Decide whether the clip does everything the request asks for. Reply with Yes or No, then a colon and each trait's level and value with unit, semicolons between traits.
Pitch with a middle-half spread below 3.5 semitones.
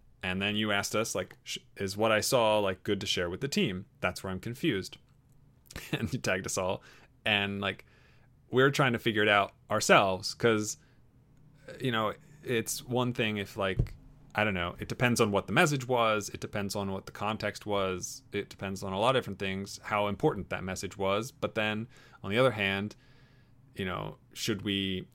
No: average, 4.0 semitones